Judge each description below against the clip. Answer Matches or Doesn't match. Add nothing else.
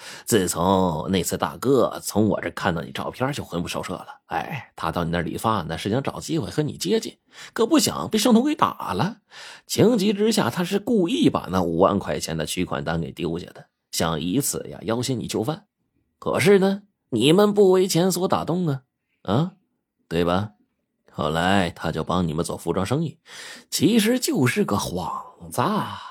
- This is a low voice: Matches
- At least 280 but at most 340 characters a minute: Doesn't match